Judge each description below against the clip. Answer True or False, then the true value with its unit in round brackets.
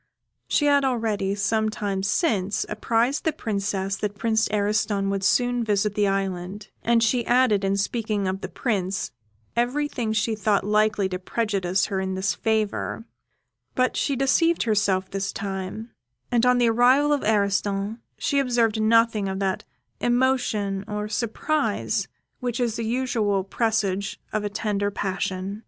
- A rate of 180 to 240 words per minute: False (155 wpm)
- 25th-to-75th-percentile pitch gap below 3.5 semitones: True (3.1 semitones)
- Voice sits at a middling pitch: False (210 Hz)